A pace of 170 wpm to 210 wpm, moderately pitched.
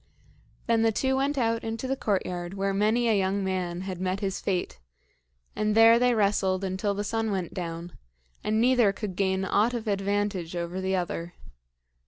No: average, 180 wpm; high, 200 Hz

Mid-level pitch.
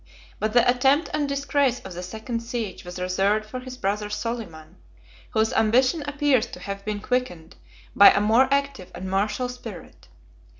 No: high, 225 Hz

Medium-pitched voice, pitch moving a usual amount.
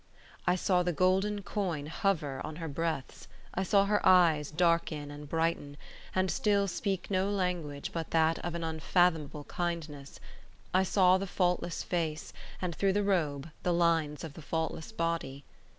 Yes: medium, 170 Hz; average, 3.2 semitones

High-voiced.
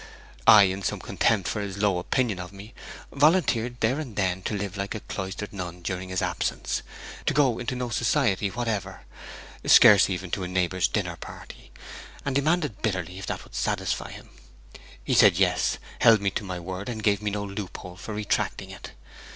No: low, 100 Hz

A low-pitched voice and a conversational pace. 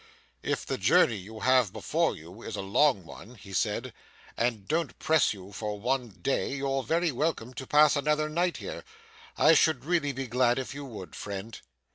Yes: low, 125 Hz; average, 185 wpm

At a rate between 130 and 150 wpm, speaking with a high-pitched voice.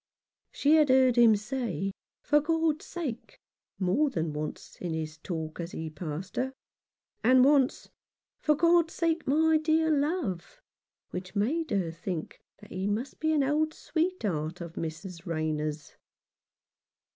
Yes: average, 145 wpm; high, 235 Hz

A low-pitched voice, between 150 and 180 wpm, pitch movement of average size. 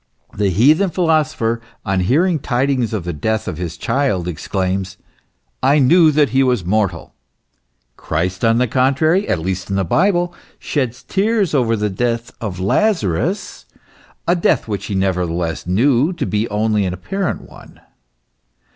No: low, 115 Hz; average, 155 wpm; wide, 7.8 semitones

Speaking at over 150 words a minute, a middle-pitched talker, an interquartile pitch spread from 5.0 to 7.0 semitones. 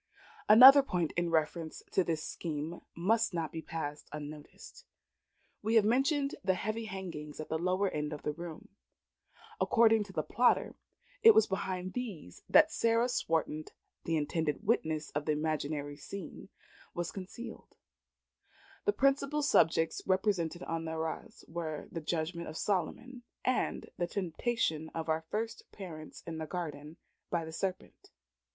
No: average, 145 wpm; medium, 170 Hz; wide, 5.6 semitones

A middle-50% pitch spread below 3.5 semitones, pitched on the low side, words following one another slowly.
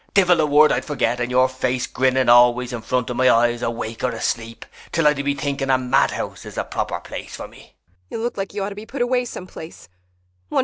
No: narrow, 2.5 semitones; low, 130 Hz; average, 175 wpm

